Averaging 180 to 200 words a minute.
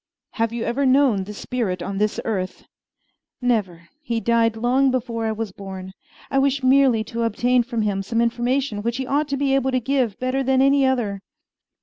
Yes: average, 195 wpm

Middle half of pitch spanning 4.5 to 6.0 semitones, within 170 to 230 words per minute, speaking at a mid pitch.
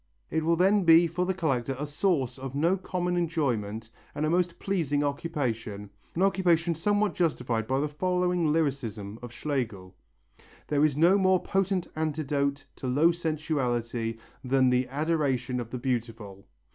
No: wide, 5.4 semitones; average, 150 wpm; medium, 150 Hz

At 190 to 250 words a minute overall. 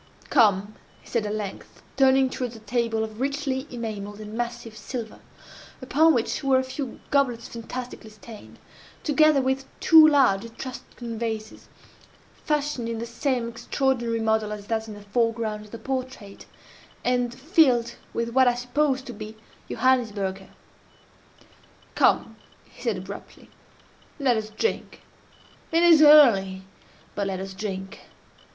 No: slow, 135 wpm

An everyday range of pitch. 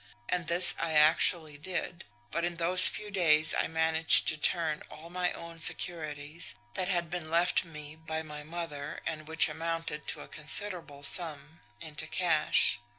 No: narrow, 2.1 semitones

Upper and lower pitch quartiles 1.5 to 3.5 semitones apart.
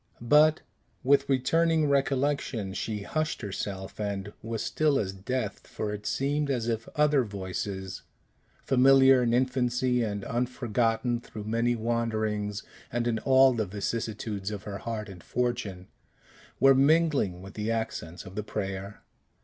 No: average, 4.3 semitones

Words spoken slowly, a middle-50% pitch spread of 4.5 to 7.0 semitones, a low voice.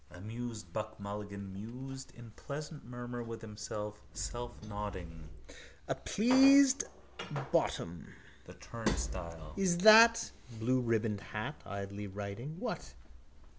Yes: slow, 95 wpm; average, 4.9 semitones; low, 110 Hz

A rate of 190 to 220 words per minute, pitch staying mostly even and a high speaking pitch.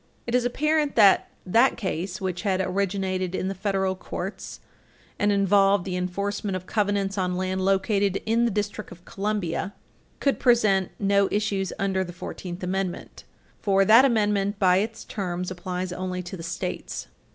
No: average, 160 wpm; narrow, 1.9 semitones; high, 195 Hz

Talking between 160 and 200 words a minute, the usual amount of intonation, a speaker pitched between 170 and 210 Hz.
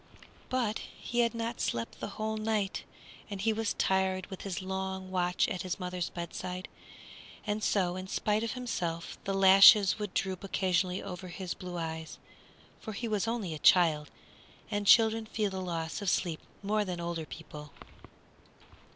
Yes: average, 165 wpm; average, 3.0 semitones; high, 190 Hz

